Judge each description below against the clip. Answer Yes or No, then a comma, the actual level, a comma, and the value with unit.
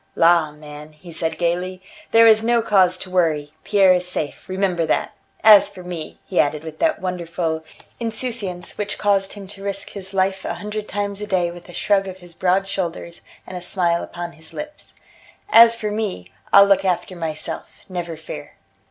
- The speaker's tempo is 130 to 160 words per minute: No, average, 185 wpm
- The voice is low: No, medium, 185 Hz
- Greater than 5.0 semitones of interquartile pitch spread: No, average, 2.9 semitones